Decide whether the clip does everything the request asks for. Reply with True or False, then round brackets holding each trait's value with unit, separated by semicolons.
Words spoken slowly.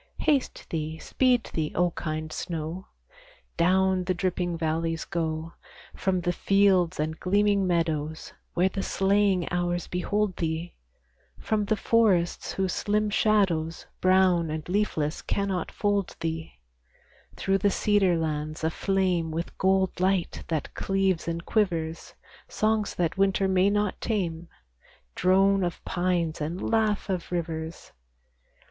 True (125 wpm)